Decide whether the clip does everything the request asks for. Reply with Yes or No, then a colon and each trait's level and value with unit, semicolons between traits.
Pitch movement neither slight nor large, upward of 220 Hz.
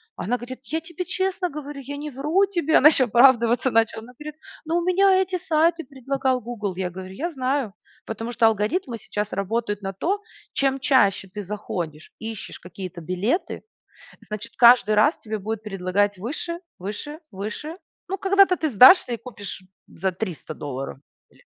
No: wide, 7.0 semitones; high, 240 Hz